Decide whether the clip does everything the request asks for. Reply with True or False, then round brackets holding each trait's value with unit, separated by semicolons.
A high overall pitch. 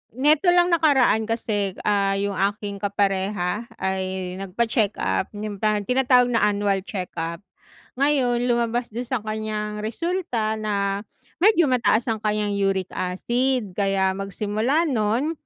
True (215 Hz)